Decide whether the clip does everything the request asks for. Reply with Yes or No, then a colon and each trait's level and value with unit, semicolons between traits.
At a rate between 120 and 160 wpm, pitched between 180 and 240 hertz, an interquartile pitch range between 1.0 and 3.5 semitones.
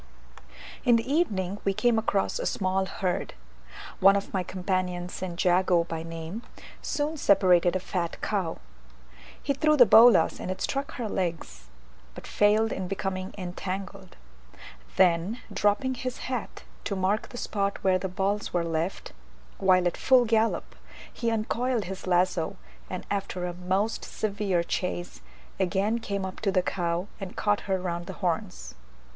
Yes: average, 155 wpm; high, 190 Hz; average, 3.0 semitones